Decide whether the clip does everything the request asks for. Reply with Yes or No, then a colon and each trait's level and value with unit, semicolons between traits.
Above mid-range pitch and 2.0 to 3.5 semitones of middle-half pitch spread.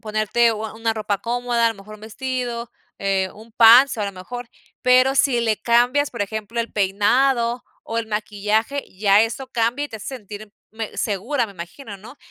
Yes: high, 225 Hz; average, 2.7 semitones